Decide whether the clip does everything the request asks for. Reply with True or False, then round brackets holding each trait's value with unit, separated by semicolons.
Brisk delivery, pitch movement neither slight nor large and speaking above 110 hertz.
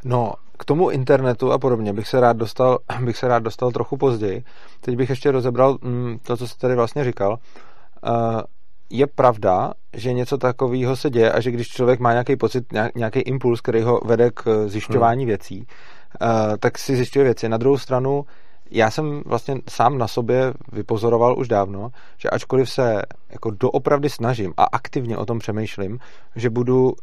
False (180 wpm; 2.2 semitones; 125 Hz)